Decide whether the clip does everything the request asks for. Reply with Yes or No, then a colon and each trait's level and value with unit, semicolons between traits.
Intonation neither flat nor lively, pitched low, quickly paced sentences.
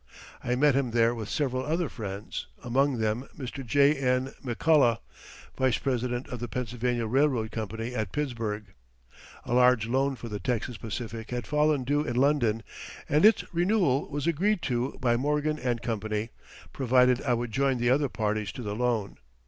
No: average, 3.3 semitones; low, 125 Hz; average, 165 wpm